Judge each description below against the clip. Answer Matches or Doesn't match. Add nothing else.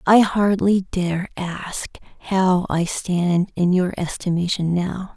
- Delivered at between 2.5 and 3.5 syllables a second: Matches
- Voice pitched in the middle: Matches